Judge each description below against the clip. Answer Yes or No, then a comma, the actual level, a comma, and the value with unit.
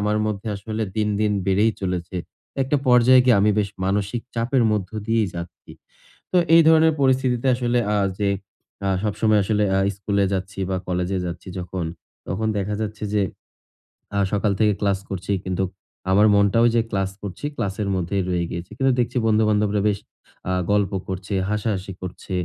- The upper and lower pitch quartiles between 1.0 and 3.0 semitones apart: Yes, narrow, 2.6 semitones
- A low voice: Yes, low, 105 Hz